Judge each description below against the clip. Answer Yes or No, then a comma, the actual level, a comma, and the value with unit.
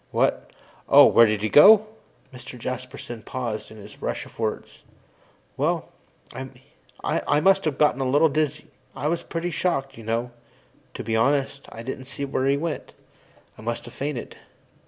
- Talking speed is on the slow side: No, average, 165 wpm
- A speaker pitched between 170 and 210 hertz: No, low, 130 Hz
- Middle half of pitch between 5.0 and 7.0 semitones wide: No, average, 4.2 semitones